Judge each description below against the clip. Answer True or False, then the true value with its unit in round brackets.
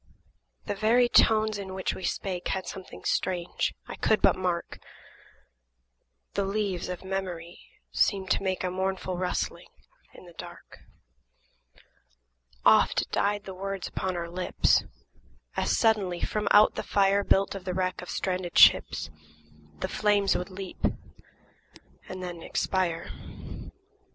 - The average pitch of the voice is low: False (190 Hz)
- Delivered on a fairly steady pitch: True (1.6 semitones)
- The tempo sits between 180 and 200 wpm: False (135 wpm)